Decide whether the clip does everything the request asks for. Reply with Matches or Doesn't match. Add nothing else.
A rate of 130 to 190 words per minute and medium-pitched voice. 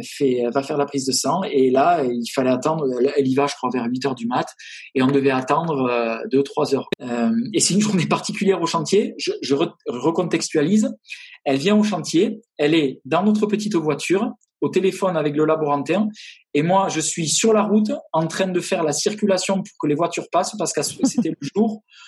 Doesn't match